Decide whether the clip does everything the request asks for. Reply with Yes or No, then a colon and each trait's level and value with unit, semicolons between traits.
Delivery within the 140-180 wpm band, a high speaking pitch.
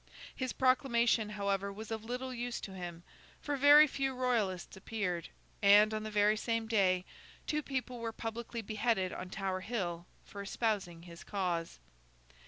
Yes: average, 155 wpm; high, 215 Hz